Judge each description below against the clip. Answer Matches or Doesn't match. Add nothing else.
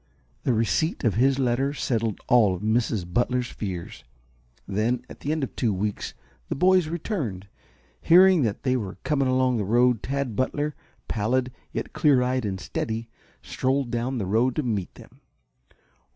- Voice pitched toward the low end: Matches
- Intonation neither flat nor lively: Matches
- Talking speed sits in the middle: Matches